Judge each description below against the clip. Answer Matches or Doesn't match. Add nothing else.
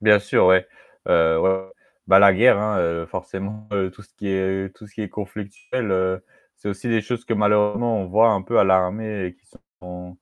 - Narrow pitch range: Matches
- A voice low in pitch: Matches